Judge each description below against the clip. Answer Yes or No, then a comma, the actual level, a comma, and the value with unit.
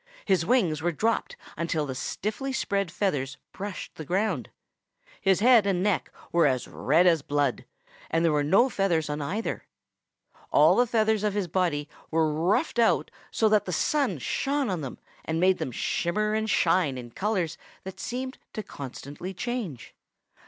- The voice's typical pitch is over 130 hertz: Yes, medium, 185 Hz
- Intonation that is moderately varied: No, wide, 5.7 semitones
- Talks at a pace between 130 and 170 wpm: Yes, average, 165 wpm